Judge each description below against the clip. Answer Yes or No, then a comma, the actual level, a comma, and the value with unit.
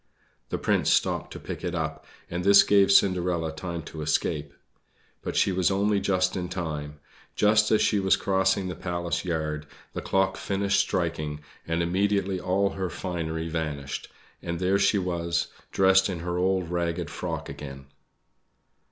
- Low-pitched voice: Yes, very low, 90 Hz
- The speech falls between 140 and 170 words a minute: Yes, average, 160 wpm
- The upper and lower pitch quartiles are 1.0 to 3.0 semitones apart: Yes, average, 2.7 semitones